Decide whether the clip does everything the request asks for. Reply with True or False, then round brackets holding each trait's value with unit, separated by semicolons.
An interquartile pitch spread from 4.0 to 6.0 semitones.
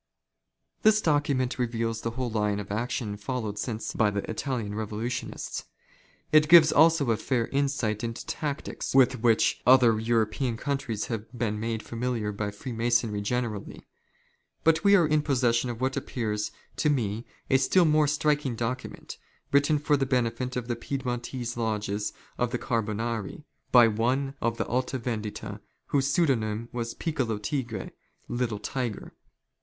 False (3.4 semitones)